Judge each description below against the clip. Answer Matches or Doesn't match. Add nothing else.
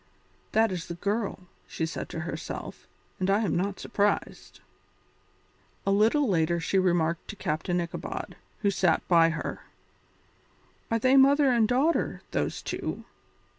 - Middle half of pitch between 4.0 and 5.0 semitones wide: Matches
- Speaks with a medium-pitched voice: Doesn't match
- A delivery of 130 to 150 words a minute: Matches